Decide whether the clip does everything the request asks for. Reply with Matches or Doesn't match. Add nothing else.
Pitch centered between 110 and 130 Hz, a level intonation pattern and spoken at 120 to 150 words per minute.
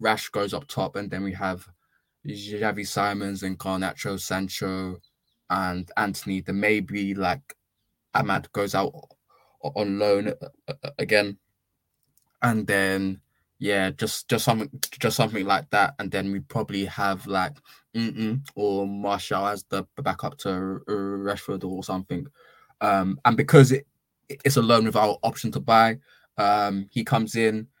Doesn't match